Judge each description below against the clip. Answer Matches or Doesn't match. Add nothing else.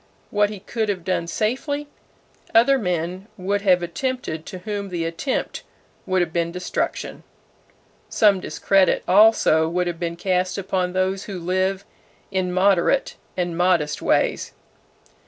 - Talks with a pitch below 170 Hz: Doesn't match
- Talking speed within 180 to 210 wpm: Doesn't match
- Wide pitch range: Doesn't match